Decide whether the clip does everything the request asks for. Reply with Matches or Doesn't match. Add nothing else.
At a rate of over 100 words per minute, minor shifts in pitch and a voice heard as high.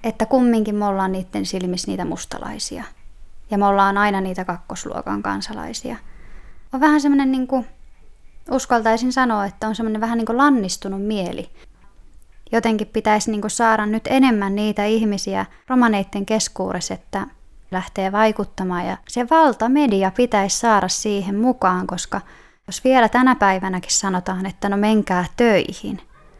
Doesn't match